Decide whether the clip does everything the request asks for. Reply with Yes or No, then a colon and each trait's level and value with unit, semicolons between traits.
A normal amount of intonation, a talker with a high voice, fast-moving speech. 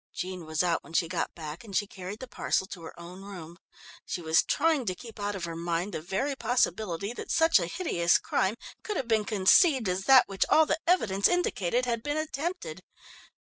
No: wide, 7.0 semitones; high, 200 Hz; fast, 210 wpm